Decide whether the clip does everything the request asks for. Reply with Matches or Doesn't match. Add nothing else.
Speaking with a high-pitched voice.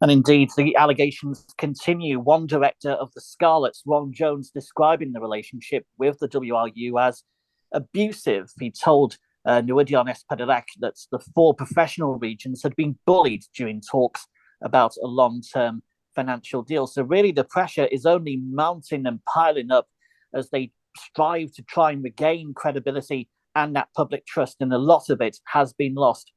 Doesn't match